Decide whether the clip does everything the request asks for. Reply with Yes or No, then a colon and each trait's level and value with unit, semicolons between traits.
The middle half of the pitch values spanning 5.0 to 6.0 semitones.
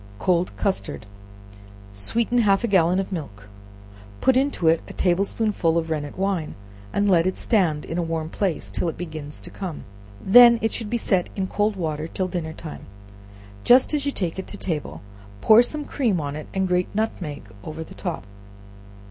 No: average, 4.5 semitones